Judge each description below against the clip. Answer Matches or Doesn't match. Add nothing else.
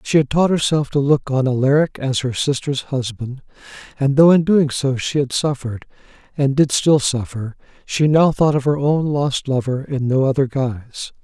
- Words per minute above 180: Matches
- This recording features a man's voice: Matches